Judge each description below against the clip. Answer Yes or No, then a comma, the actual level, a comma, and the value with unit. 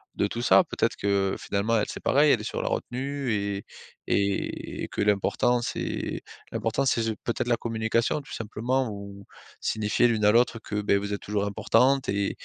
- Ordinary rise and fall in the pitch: Yes, average, 3.0 semitones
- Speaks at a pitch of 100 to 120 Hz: Yes, low, 110 Hz